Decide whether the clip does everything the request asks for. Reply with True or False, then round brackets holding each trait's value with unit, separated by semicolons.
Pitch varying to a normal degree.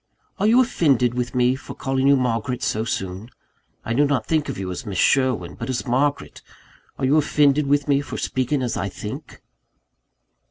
True (3.3 semitones)